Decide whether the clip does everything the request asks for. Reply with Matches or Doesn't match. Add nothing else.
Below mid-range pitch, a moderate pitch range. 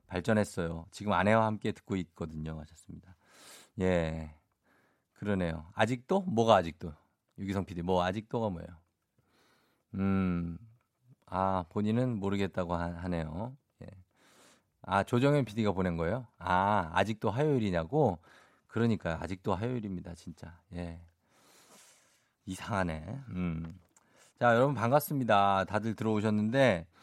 Matches